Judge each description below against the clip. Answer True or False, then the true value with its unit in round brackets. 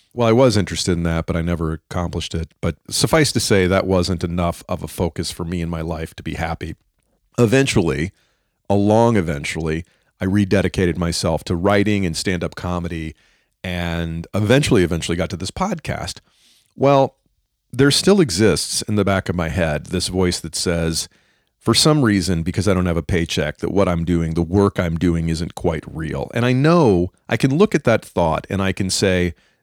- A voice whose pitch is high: False (90 Hz)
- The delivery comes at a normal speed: True (190 wpm)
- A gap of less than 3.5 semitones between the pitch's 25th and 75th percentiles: False (3.8 semitones)